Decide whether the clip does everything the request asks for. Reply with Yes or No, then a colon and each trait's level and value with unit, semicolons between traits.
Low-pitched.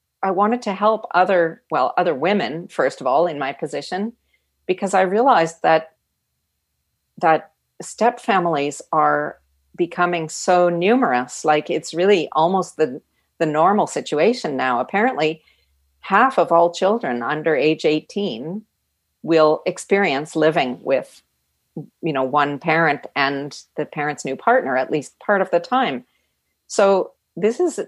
No: medium, 165 Hz